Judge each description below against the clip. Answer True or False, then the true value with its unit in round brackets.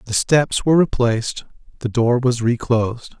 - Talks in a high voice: False (120 Hz)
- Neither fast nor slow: True (150 wpm)